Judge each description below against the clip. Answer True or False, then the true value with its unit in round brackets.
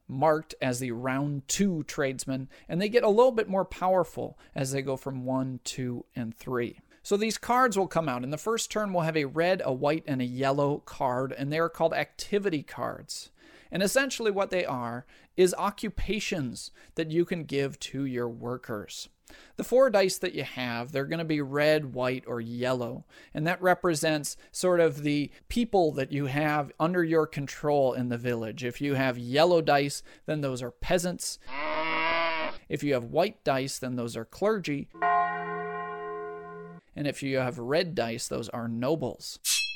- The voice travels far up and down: True (5.7 semitones)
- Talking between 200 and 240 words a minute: False (180 wpm)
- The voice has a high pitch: False (145 Hz)